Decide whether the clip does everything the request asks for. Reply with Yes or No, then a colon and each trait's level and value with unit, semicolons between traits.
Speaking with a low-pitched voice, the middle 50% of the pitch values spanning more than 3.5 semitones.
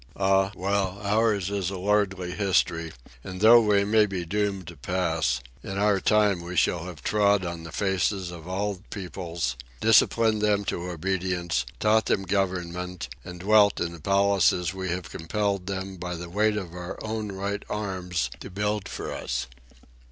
No: very low, 95 Hz; narrow, 2.5 semitones